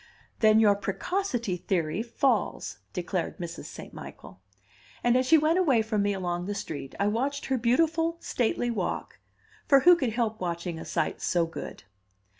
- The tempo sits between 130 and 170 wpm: Yes, average, 165 wpm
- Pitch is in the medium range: No, high, 220 Hz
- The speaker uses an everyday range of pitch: No, wide, 6.6 semitones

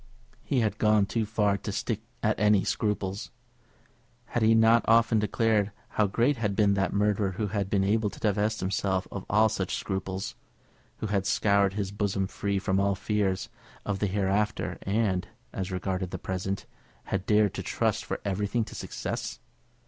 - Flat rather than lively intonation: Yes, narrow, 1.8 semitones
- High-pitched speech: No, low, 100 Hz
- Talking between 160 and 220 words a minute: Yes, average, 170 wpm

